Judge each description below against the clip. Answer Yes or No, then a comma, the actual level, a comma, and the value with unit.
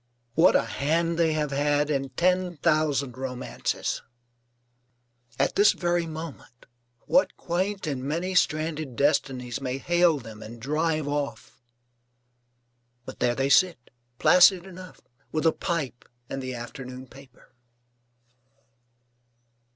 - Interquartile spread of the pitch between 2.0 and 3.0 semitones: No, average, 4.2 semitones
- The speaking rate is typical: No, slow, 120 wpm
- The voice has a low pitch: No, medium, 150 Hz